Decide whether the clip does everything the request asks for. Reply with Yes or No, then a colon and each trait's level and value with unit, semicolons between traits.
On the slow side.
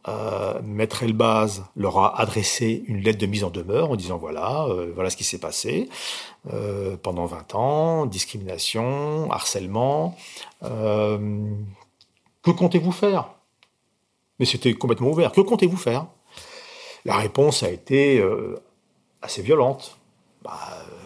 Yes: slow, 135 wpm